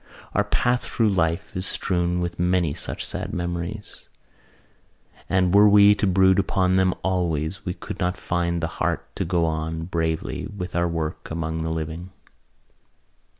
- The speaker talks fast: No, average, 155 wpm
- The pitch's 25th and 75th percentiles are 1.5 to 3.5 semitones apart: Yes, narrow, 2.4 semitones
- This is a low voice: Yes, very low, 90 Hz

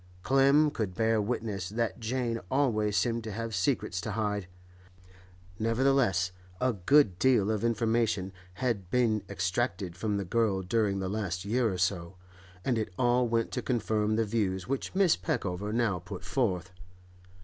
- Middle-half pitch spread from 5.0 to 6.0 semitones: No, average, 3.8 semitones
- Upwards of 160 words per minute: No, average, 155 wpm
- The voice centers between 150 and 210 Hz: No, low, 110 Hz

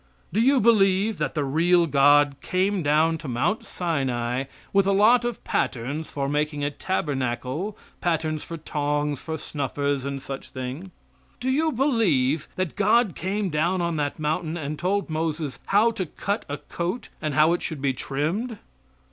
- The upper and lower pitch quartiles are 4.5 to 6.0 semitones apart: Yes, average, 5.3 semitones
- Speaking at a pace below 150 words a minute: No, average, 165 wpm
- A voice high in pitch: No, medium, 160 Hz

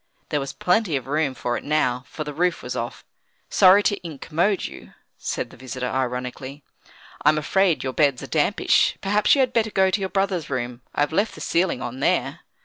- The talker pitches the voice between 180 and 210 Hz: No, medium, 155 Hz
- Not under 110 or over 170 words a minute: No, average, 200 wpm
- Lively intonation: Yes, wide, 6.5 semitones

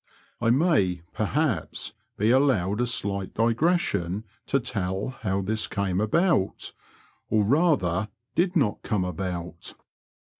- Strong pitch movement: Yes, wide, 5.8 semitones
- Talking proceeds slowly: Yes, slow, 125 wpm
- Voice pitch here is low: Yes, low, 105 Hz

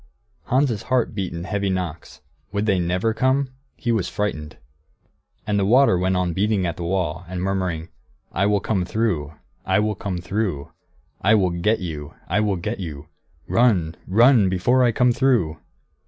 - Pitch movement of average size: Yes, average, 4.1 semitones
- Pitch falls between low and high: No, very low, 95 Hz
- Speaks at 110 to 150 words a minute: No, average, 170 wpm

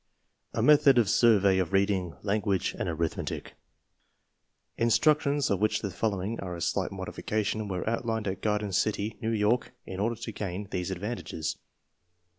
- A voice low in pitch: Yes, low, 105 Hz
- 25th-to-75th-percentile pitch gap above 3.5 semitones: No, average, 3.2 semitones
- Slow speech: No, average, 150 wpm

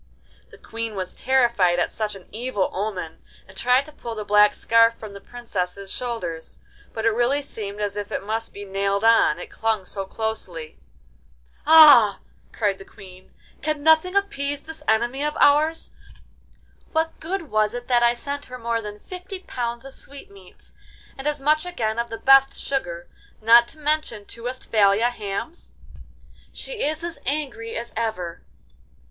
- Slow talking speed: No, average, 165 wpm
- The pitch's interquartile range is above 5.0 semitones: Yes, wide, 5.5 semitones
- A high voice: Yes, high, 230 Hz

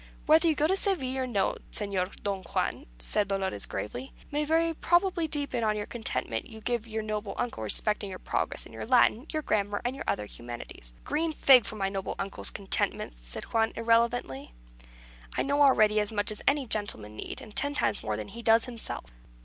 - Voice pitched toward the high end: Yes, high, 220 Hz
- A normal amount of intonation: No, wide, 5.7 semitones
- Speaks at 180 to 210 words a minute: Yes, average, 200 wpm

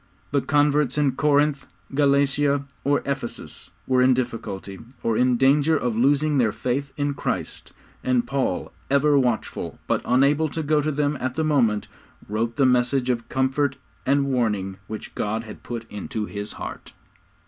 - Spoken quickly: No, average, 160 wpm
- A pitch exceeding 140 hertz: No, low, 135 Hz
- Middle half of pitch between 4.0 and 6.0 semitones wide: No, average, 3.3 semitones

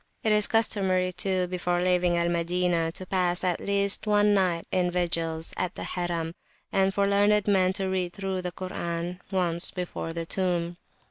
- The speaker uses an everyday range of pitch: No, narrow, 1.9 semitones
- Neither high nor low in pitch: Yes, medium, 180 Hz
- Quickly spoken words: No, average, 175 wpm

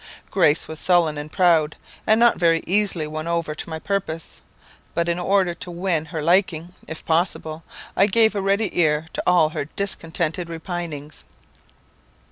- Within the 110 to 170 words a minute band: Yes, average, 160 wpm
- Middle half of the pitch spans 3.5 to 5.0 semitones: No, average, 2.7 semitones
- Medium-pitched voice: Yes, medium, 170 Hz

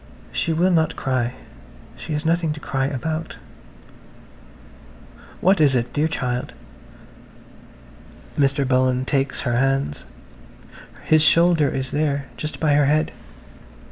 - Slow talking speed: Yes, slow, 110 wpm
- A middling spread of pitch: Yes, average, 3.4 semitones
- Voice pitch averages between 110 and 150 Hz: Yes, medium, 140 Hz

